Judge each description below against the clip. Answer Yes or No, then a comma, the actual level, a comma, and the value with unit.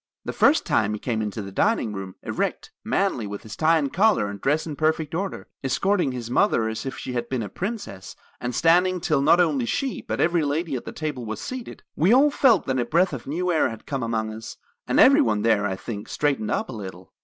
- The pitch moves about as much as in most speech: No, wide, 7.9 semitones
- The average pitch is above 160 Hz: No, low, 135 Hz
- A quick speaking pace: Yes, fast, 235 wpm